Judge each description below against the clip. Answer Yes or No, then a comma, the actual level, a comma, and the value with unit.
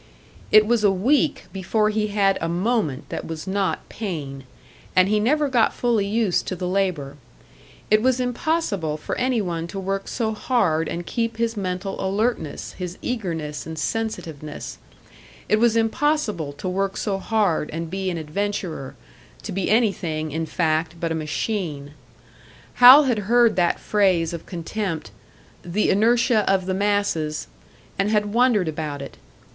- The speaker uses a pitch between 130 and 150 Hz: No, high, 195 Hz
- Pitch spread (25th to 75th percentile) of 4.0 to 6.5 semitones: Yes, average, 5.1 semitones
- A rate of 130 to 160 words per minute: Yes, average, 155 wpm